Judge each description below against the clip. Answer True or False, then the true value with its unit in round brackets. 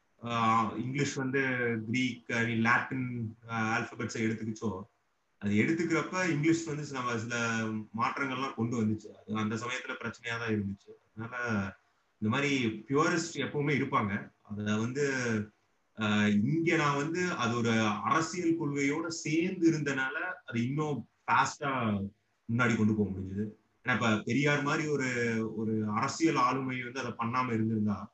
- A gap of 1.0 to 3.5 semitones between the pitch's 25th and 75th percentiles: False (4.2 semitones)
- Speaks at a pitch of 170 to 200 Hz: False (120 Hz)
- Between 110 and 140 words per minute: True (120 wpm)